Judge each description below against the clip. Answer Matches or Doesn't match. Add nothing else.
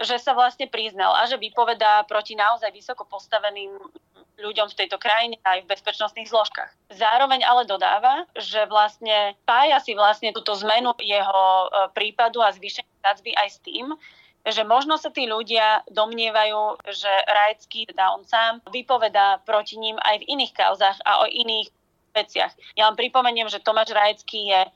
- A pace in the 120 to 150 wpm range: Doesn't match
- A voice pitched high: Matches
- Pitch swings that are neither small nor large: Doesn't match